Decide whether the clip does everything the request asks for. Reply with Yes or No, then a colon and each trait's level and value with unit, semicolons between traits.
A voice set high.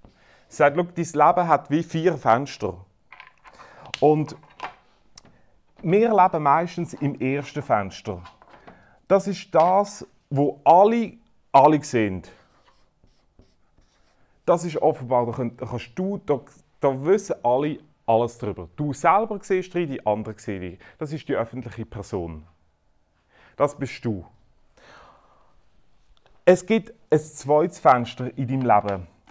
No: medium, 140 Hz